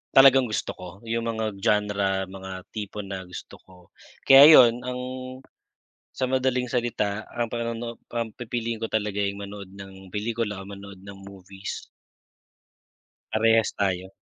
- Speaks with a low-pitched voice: Yes, low, 105 Hz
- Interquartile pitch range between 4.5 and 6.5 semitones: No, average, 3.0 semitones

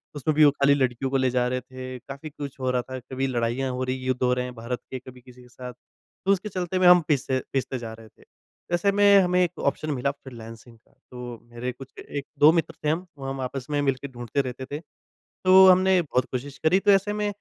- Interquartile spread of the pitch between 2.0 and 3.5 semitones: No, average, 3.9 semitones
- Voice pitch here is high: No, low, 135 Hz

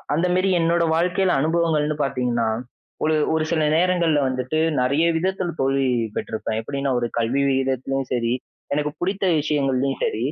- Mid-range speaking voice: Yes, medium, 145 Hz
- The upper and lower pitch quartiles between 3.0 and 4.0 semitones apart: No, average, 4.4 semitones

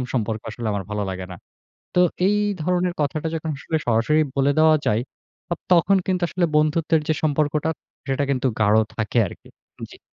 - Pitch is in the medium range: Yes, medium, 150 Hz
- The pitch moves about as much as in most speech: No, wide, 6.0 semitones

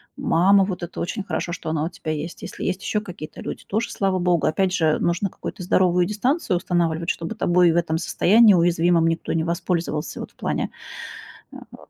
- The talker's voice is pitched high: No, medium, 175 Hz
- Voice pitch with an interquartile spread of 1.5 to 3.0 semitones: Yes, narrow, 2.4 semitones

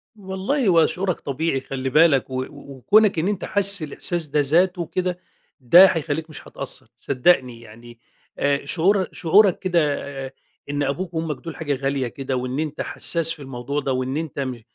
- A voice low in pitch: No, medium, 150 Hz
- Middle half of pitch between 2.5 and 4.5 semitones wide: No, average, 4.9 semitones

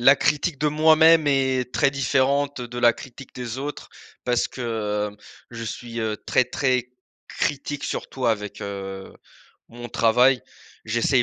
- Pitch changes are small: No, average, 3.1 semitones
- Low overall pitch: Yes, low, 125 Hz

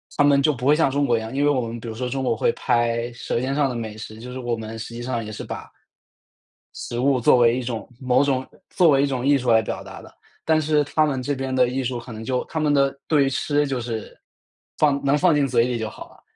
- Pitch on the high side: No, low, 130 Hz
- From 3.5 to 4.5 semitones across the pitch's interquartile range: No, average, 3.1 semitones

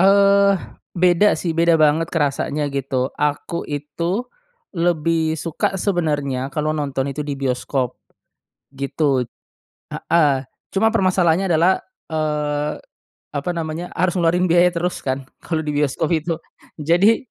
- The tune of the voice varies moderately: Yes, average, 3.2 semitones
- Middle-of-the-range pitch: Yes, medium, 160 Hz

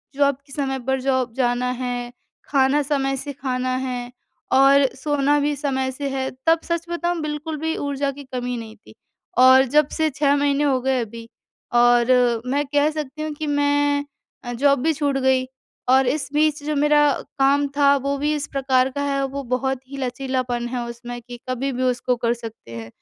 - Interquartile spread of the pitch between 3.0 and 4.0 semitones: No, narrow, 2.4 semitones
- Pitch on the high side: Yes, very high, 270 Hz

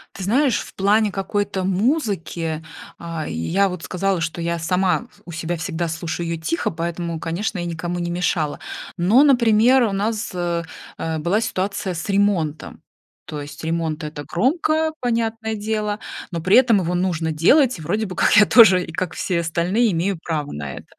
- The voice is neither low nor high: Yes, medium, 180 Hz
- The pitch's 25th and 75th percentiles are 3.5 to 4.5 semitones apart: Yes, average, 4.2 semitones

